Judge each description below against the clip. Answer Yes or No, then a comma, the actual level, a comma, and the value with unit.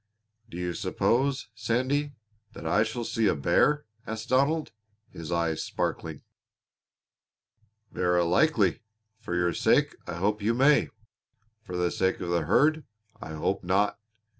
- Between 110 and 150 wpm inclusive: Yes, average, 140 wpm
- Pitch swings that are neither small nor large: No, wide, 6.8 semitones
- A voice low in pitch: Yes, low, 105 Hz